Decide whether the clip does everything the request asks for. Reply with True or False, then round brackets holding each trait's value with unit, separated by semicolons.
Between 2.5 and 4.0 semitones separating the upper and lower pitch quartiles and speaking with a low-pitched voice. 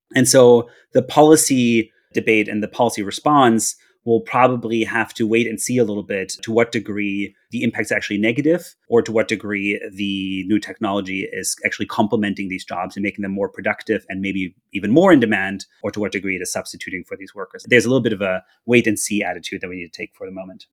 True (2.9 semitones; 110 Hz)